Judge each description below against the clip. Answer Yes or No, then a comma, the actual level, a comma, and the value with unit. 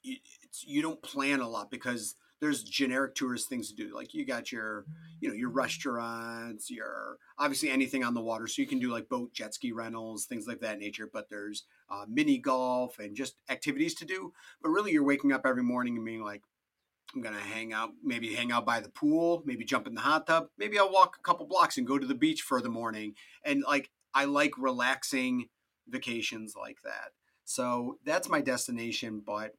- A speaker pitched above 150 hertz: No, low, 135 Hz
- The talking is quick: Yes, fast, 210 wpm